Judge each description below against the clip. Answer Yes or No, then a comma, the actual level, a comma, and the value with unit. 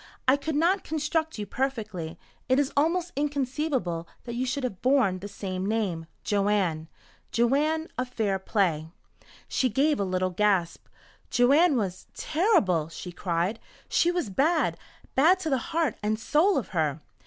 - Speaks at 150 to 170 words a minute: Yes, average, 155 wpm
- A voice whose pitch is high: Yes, high, 240 Hz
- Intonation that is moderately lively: No, wide, 7.9 semitones